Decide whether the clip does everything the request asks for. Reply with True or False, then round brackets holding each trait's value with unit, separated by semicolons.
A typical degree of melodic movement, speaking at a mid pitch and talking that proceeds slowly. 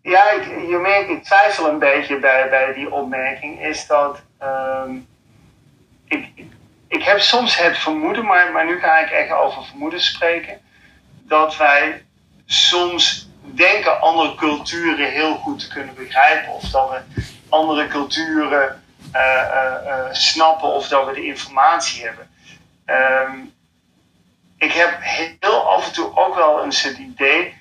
False (4.2 semitones; 150 Hz; 150 wpm)